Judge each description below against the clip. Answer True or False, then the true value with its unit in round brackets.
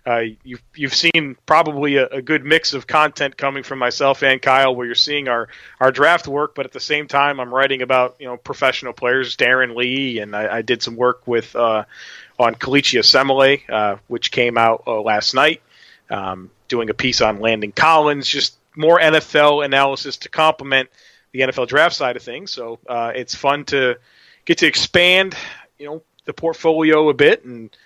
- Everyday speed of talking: True (190 wpm)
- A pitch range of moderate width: True (3.4 semitones)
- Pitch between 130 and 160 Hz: True (135 Hz)